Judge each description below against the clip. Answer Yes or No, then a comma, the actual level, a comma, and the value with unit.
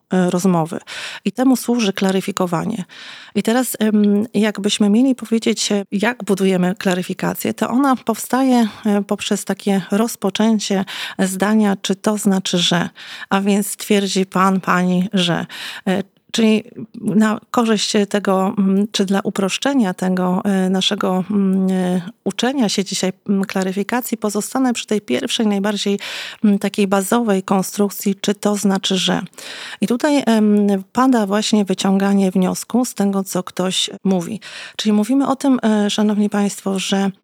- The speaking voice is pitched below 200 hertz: No, high, 205 Hz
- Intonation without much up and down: Yes, narrow, 2.3 semitones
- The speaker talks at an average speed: Yes, average, 120 wpm